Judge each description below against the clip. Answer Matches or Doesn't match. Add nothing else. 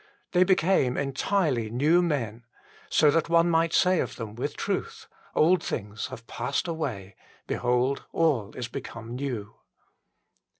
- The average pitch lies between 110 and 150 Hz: Matches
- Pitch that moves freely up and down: Matches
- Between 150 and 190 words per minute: Doesn't match